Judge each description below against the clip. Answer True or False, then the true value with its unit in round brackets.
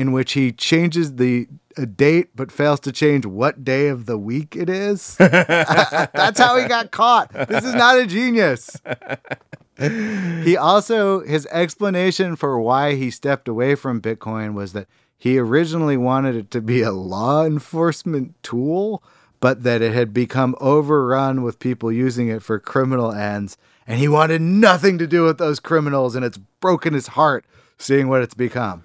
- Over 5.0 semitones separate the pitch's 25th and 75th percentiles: True (5.5 semitones)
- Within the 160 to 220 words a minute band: True (170 wpm)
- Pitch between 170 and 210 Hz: False (140 Hz)